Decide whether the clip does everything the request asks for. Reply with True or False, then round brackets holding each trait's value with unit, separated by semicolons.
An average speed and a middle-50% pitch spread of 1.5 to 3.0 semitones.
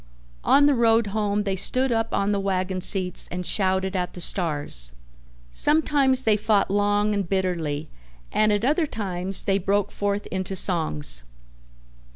True (155 wpm; 2.7 semitones)